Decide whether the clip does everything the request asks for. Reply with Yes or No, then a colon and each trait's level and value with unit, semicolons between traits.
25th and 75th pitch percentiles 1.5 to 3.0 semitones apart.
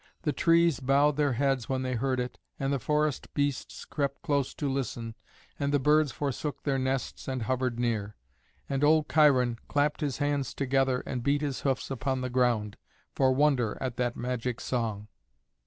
Yes: narrow, 2.4 semitones